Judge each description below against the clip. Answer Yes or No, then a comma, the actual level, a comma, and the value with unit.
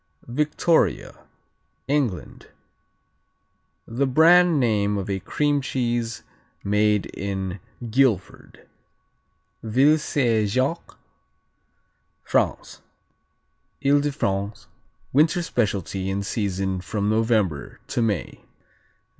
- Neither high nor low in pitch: No, low, 110 Hz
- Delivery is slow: Yes, slow, 85 wpm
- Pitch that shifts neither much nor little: No, wide, 5.8 semitones